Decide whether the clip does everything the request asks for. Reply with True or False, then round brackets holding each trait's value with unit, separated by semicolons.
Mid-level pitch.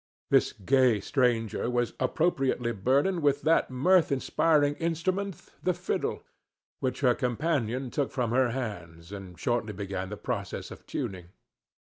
False (125 Hz)